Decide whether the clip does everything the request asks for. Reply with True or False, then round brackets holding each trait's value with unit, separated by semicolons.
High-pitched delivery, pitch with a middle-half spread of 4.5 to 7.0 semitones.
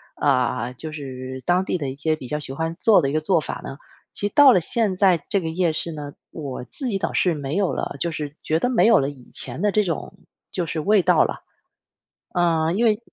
False (160 Hz; 5.1 semitones)